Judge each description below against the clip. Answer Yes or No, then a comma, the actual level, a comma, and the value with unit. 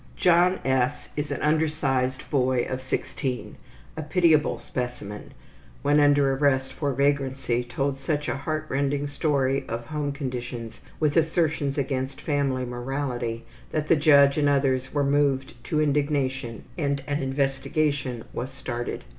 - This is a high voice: No, medium, 140 Hz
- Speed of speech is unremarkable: No, slow, 130 wpm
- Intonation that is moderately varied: No, narrow, 2.0 semitones